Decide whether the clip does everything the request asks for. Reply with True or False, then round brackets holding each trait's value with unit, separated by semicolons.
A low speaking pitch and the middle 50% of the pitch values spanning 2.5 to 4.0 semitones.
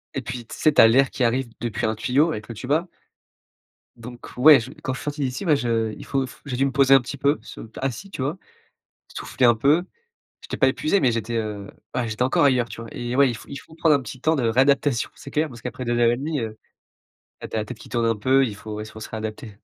True (125 Hz; 3.4 semitones)